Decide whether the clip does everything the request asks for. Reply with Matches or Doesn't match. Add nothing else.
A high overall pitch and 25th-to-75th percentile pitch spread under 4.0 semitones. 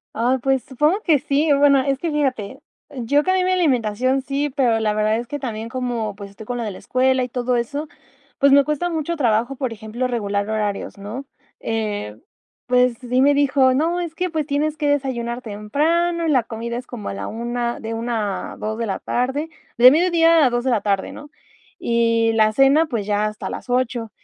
Doesn't match